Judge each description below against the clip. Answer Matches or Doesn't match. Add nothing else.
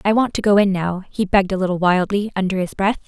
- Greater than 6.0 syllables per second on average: Matches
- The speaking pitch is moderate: Doesn't match